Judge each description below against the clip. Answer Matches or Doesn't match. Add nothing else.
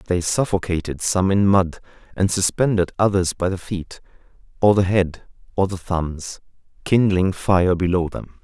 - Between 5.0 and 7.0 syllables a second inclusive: Doesn't match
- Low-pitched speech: Matches